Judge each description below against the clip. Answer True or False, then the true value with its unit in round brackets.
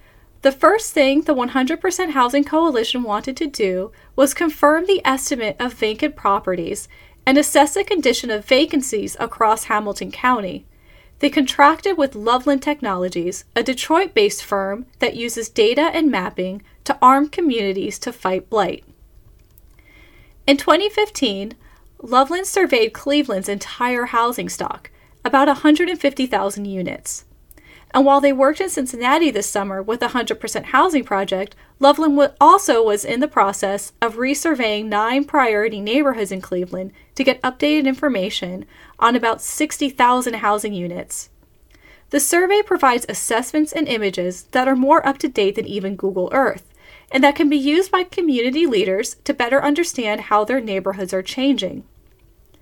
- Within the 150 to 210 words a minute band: False (140 wpm)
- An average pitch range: False (5.9 semitones)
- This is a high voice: True (260 Hz)